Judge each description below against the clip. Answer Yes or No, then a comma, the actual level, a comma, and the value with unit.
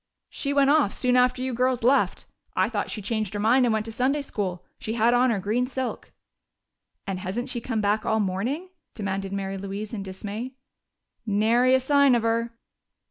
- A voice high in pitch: Yes, high, 230 Hz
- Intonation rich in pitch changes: No, average, 3.8 semitones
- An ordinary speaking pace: Yes, average, 190 wpm